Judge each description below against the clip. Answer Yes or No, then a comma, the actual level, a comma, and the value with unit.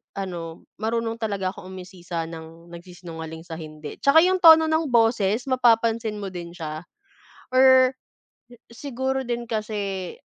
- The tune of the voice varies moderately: No, wide, 5.9 semitones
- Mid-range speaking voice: No, high, 210 Hz